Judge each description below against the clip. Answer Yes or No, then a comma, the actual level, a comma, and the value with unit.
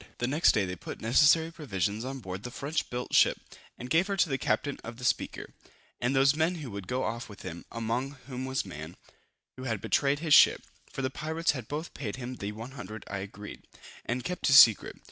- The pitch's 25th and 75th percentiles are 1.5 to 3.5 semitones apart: No, average, 4.9 semitones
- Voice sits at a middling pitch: No, low, 125 Hz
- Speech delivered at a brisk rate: Yes, fast, 215 wpm